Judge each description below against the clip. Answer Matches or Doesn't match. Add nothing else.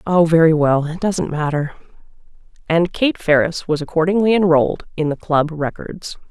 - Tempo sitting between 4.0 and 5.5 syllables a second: Matches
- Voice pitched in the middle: Matches